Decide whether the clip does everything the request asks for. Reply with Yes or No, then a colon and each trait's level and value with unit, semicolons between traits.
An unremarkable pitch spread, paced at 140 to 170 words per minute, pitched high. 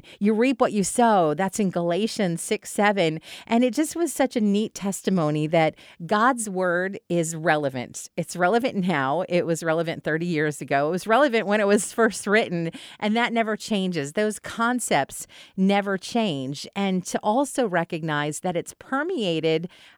Yes: average, 5.0 semitones; average, 165 wpm; high, 195 Hz